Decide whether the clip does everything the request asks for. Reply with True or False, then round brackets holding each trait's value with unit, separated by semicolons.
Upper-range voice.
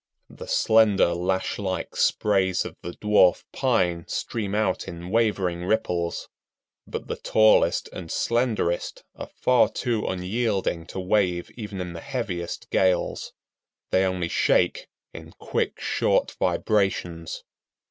False (95 Hz)